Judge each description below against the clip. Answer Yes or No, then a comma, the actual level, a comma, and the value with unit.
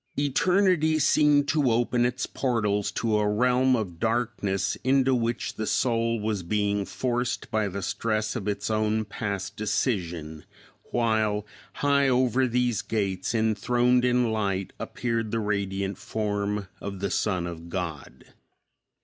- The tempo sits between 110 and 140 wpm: Yes, slow, 135 wpm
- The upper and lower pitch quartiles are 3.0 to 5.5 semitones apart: Yes, average, 3.5 semitones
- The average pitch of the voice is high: No, low, 110 Hz